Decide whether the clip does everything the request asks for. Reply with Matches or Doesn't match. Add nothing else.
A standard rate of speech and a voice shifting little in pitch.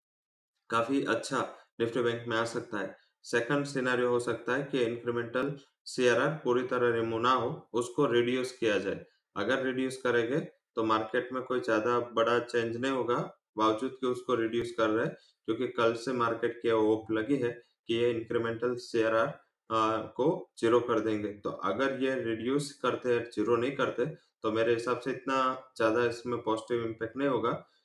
Matches